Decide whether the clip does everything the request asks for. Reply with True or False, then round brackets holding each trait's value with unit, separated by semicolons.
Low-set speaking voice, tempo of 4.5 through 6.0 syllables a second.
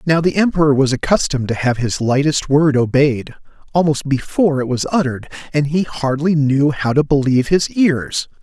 False (145 Hz; 5.3 syllables/s)